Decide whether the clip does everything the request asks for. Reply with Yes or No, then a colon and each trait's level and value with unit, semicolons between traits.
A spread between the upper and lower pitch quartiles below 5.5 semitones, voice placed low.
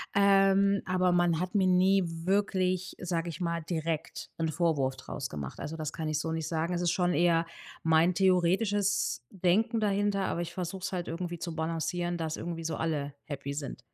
No: average, 2.7 semitones; medium, 175 Hz